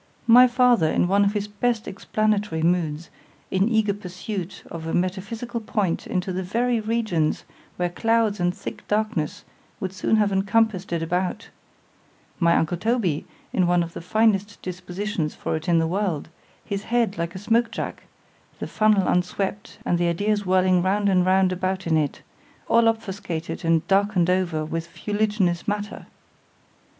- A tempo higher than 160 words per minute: No, average, 150 wpm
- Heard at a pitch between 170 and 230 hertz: Yes, high, 190 Hz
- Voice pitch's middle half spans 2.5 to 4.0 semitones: Yes, average, 3.4 semitones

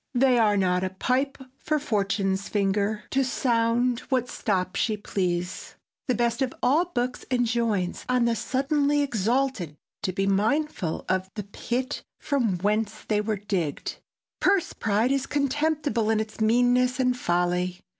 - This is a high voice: Yes, high, 230 Hz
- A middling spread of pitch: Yes, average, 4.6 semitones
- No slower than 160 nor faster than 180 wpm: No, average, 145 wpm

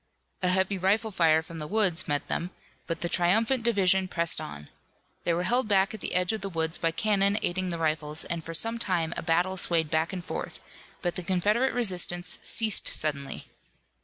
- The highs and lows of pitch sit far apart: No, average, 3.3 semitones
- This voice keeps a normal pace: Yes, average, 195 wpm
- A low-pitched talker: No, medium, 180 Hz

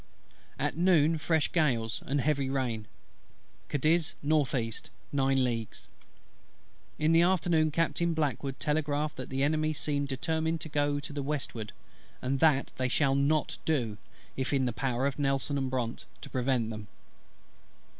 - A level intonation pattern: No, average, 3.0 semitones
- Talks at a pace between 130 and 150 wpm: Yes, average, 145 wpm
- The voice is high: No, medium, 140 Hz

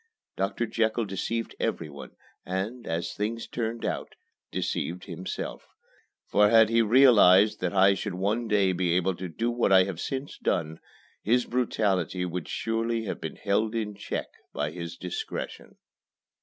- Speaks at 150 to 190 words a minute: Yes, average, 155 wpm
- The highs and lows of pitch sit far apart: No, average, 4.0 semitones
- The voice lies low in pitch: Yes, low, 100 Hz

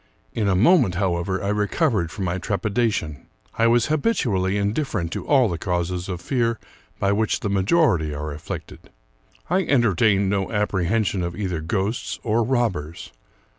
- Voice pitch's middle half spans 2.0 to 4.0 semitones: No, average, 4.5 semitones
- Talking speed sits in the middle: Yes, average, 160 wpm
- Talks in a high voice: No, low, 100 Hz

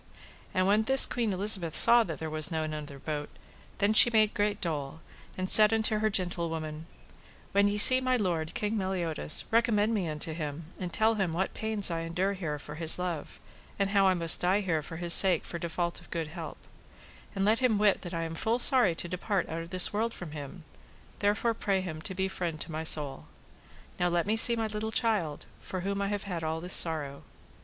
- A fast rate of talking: Yes, fast, 215 wpm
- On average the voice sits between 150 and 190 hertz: Yes, medium, 185 Hz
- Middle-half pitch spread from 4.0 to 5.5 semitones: Yes, average, 4.4 semitones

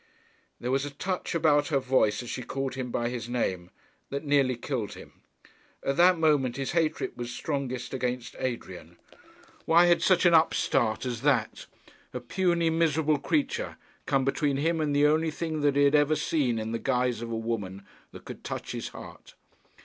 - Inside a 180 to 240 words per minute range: Yes, average, 185 wpm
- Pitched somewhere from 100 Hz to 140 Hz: Yes, low, 135 Hz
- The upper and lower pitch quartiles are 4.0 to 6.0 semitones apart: Yes, average, 4.4 semitones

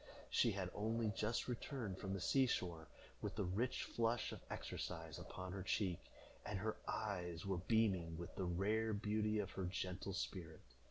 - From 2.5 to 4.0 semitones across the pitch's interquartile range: Yes, average, 3.3 semitones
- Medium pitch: No, low, 100 Hz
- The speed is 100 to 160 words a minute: No, average, 170 wpm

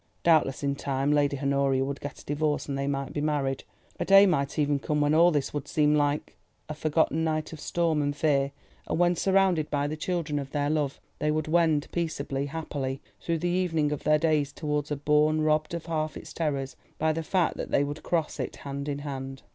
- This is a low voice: No, medium, 150 Hz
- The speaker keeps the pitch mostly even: Yes, narrow, 2.0 semitones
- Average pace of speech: No, fast, 215 wpm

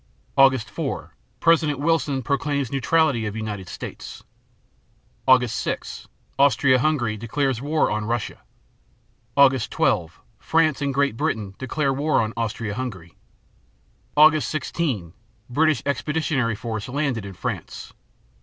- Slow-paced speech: Yes, slow, 115 wpm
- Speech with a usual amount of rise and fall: Yes, average, 4.8 semitones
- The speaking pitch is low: Yes, low, 130 Hz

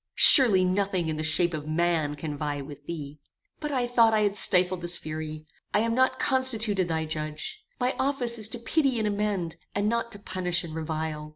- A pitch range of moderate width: No, wide, 6.4 semitones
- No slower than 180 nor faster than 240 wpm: Yes, average, 200 wpm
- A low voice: No, medium, 185 Hz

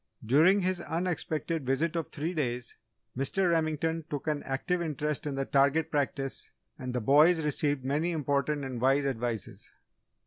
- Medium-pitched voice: Yes, medium, 145 Hz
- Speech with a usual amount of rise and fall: Yes, average, 3.2 semitones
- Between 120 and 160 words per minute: Yes, average, 150 wpm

